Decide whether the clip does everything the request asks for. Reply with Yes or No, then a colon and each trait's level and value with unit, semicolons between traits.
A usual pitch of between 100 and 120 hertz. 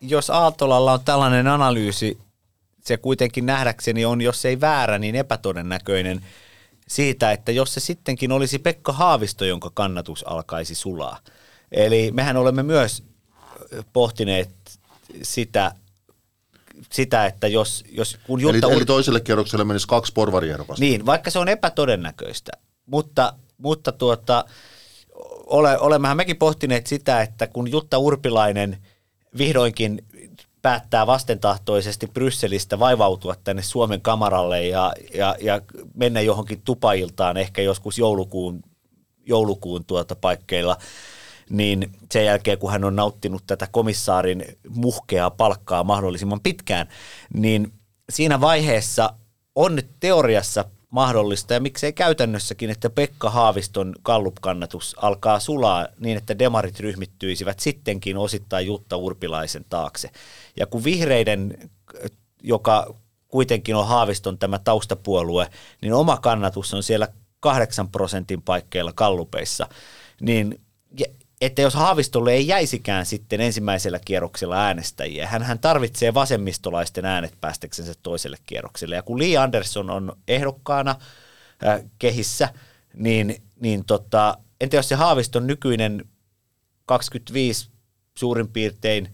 Yes: low, 110 Hz